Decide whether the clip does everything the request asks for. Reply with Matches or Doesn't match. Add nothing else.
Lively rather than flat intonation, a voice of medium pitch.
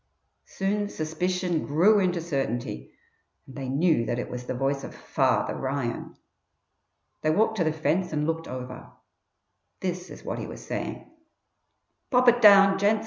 Matches